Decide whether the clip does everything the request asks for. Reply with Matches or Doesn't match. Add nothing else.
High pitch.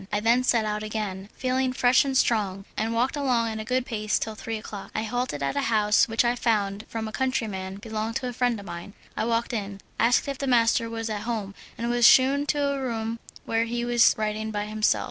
Matches